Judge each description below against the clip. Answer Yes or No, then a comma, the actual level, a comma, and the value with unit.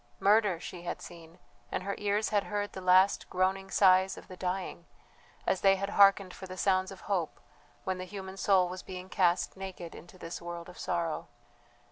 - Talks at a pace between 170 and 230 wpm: Yes, average, 190 wpm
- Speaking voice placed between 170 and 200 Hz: Yes, medium, 185 Hz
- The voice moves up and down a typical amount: No, narrow, 1.5 semitones